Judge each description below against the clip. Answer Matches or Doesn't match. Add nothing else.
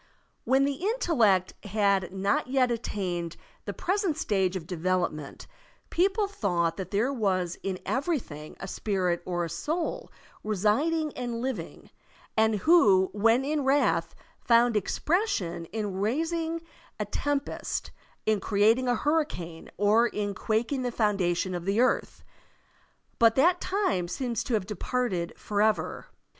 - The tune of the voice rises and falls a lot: Matches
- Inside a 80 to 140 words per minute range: Matches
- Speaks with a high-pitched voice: Matches